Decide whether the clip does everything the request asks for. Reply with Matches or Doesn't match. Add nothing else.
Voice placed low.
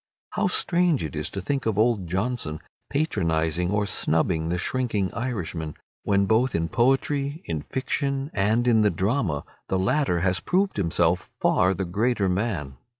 Matches